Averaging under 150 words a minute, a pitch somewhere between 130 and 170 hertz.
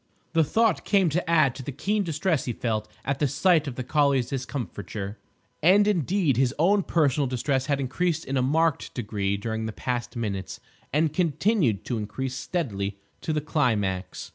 No: average, 175 wpm; medium, 140 Hz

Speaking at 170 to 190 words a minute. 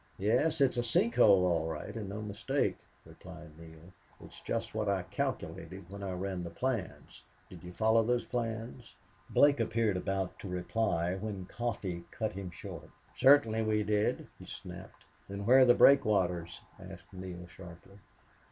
No: average, 160 wpm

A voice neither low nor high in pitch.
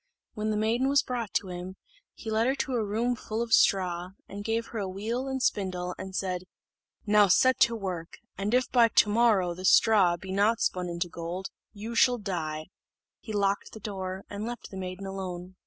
No: high, 200 Hz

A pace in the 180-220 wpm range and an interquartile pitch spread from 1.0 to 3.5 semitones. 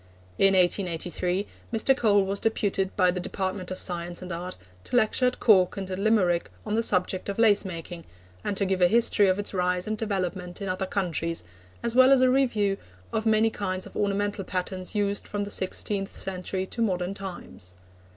Yes: average, 195 wpm; narrow, 2.5 semitones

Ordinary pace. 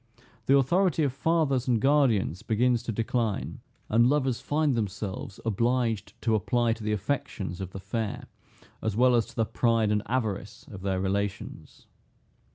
Yes: average, 160 wpm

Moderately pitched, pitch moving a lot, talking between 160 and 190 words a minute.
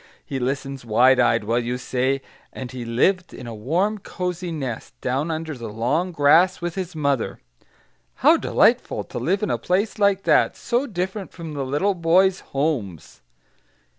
Yes: medium, 150 Hz; wide, 6.2 semitones; average, 165 wpm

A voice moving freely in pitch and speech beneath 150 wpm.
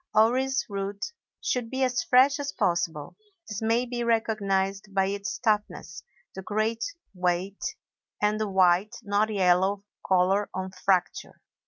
No: average, 3.2 semitones; slow, 135 wpm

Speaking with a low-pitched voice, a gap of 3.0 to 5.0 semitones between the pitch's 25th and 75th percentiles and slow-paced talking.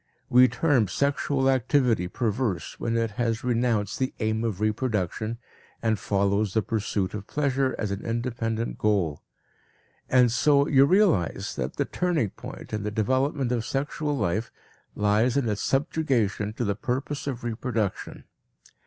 No: low, 115 Hz; average, 3.9 semitones; average, 145 wpm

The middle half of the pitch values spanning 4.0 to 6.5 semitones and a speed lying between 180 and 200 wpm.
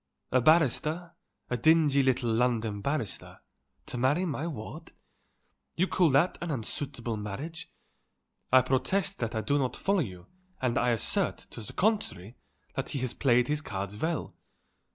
No: wide, 5.4 semitones; average, 155 wpm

